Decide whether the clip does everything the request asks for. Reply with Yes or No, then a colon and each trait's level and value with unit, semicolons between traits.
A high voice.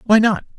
Yes: high, 220 Hz